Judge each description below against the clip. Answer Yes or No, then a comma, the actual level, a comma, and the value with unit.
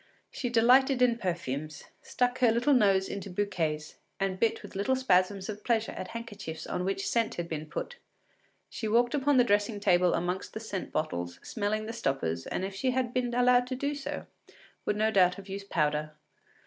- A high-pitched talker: Yes, high, 205 Hz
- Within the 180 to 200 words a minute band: Yes, average, 190 wpm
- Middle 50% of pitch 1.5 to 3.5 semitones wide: No, average, 5.1 semitones